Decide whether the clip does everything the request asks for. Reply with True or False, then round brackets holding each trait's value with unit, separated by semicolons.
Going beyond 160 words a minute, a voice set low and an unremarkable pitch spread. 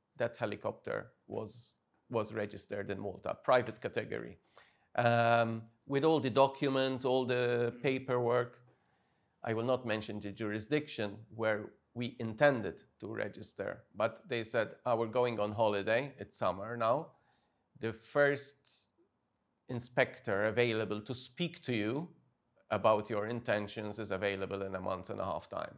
False (135 wpm; 115 Hz; 3.2 semitones)